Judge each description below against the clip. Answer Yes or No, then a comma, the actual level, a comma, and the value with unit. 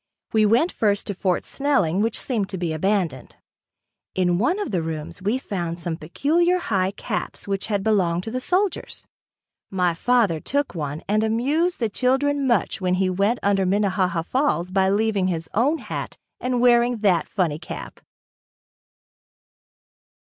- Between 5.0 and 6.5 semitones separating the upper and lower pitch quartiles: Yes, wide, 5.4 semitones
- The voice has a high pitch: Yes, high, 200 Hz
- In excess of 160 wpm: No, average, 155 wpm